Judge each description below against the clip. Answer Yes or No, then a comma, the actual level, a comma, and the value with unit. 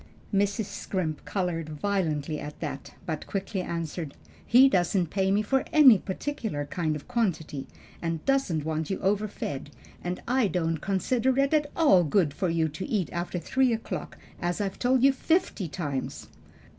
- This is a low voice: No, medium, 185 Hz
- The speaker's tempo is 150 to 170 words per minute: Yes, average, 155 wpm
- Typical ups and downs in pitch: No, wide, 5.9 semitones